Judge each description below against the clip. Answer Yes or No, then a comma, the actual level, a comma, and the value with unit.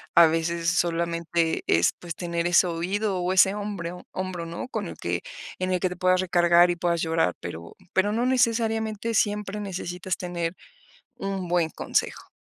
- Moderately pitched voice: Yes, medium, 180 Hz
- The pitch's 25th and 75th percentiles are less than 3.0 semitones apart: Yes, narrow, 2.6 semitones